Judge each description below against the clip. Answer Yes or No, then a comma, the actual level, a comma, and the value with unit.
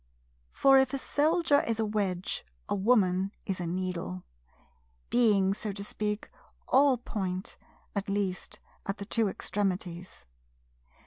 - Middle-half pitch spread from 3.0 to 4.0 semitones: Yes, average, 3.6 semitones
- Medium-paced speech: No, slow, 130 wpm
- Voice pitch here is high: Yes, high, 200 Hz